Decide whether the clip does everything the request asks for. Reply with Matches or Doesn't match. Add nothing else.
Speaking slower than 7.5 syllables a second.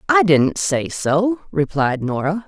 Matches